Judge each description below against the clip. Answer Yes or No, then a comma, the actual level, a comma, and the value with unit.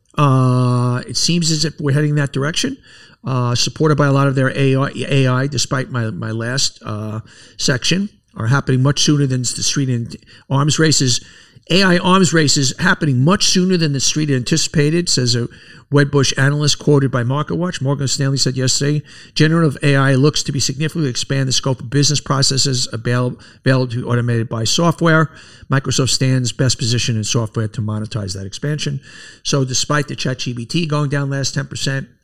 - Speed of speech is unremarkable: Yes, average, 175 wpm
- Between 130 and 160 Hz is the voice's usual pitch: Yes, low, 135 Hz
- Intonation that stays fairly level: No, average, 3.1 semitones